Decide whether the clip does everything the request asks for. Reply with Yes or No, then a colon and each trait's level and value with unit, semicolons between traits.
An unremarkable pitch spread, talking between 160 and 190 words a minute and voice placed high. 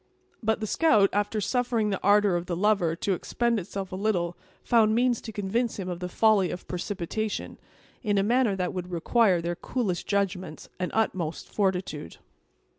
Yes: average, 3.4 semitones; average, 175 wpm; high, 200 Hz